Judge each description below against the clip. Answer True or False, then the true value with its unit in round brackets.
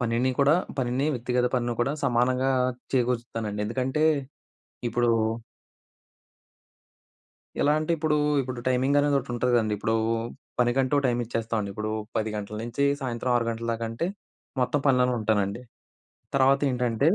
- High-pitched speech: False (125 Hz)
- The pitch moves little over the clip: True (2.3 semitones)